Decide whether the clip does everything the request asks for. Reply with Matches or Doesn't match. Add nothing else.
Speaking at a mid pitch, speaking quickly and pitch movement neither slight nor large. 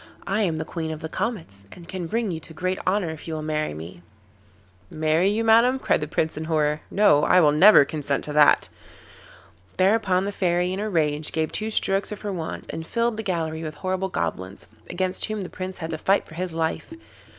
Matches